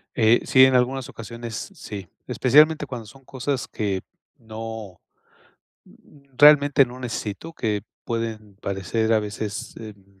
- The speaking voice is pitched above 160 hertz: No, low, 115 Hz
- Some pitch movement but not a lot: Yes, average, 3.7 semitones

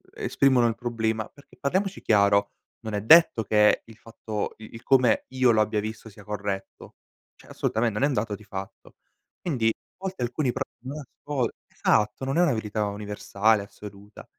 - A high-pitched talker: No, low, 110 Hz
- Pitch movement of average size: Yes, average, 3.7 semitones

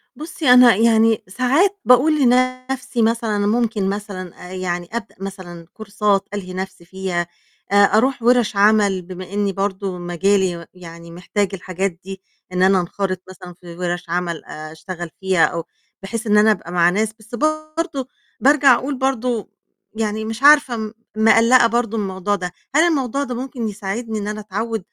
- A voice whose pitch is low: No, high, 205 Hz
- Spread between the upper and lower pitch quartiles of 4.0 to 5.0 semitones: Yes, average, 4.5 semitones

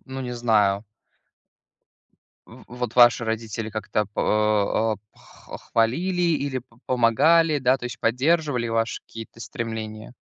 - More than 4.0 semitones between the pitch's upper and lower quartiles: No, average, 2.8 semitones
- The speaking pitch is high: No, low, 115 Hz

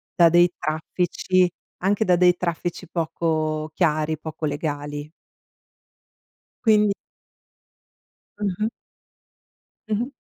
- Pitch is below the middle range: No, medium, 170 Hz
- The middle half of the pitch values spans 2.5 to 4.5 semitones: Yes, average, 2.9 semitones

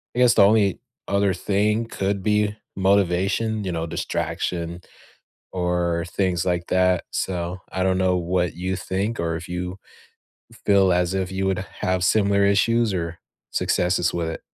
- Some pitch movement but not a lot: No, narrow, 2.2 semitones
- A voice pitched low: Yes, very low, 95 Hz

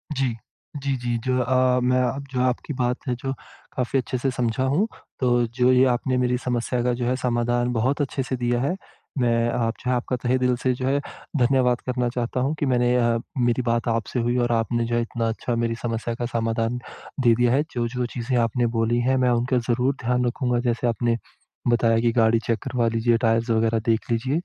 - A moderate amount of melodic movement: No, narrow, 1.4 semitones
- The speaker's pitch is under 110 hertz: No, low, 120 Hz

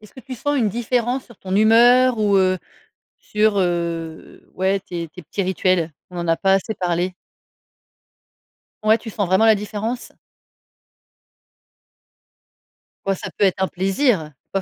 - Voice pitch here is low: No, high, 195 Hz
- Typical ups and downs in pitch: Yes, average, 3.4 semitones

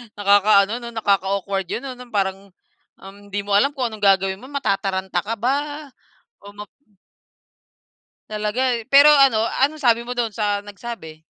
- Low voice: No, high, 210 Hz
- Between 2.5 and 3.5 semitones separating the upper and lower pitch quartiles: No, average, 3.9 semitones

